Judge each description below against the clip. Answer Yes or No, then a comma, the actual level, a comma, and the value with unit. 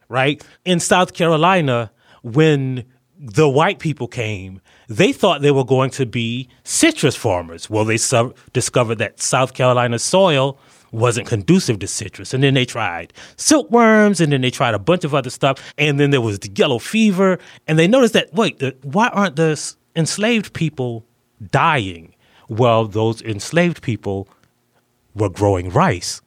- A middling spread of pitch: No, wide, 5.8 semitones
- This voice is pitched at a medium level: No, low, 130 Hz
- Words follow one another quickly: No, average, 155 wpm